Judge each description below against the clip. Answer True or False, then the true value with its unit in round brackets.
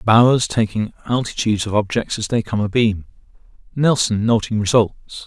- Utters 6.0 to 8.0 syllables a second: False (5.1 syllables/s)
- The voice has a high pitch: False (110 Hz)